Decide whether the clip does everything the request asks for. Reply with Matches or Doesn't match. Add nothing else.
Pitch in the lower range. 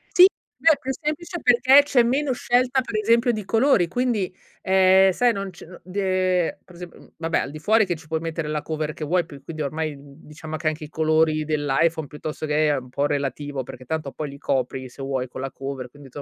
Doesn't match